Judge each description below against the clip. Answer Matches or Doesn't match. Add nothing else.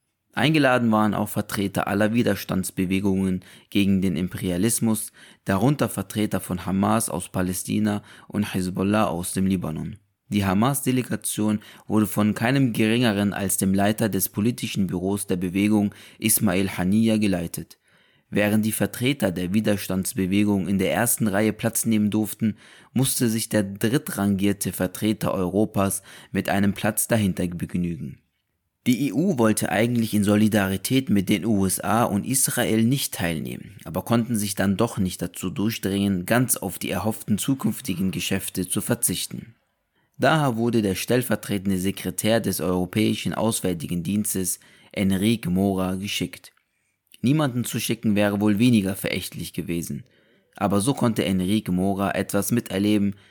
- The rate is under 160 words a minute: Matches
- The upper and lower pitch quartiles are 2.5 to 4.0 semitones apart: Matches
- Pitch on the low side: Matches